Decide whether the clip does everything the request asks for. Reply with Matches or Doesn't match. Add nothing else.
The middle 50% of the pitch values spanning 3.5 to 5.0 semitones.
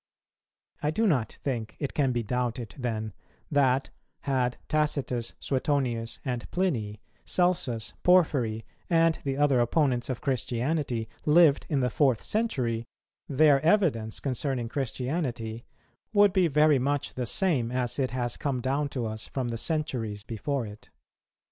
Matches